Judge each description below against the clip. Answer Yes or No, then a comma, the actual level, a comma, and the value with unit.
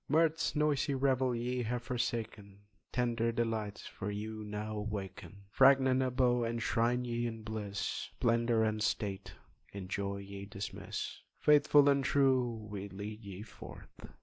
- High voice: No, low, 115 Hz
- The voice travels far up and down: No, average, 3.4 semitones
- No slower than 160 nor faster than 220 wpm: No, slow, 135 wpm